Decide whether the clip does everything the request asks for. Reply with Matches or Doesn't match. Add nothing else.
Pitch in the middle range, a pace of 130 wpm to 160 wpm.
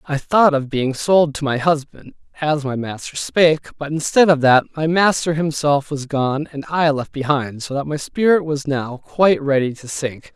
Doesn't match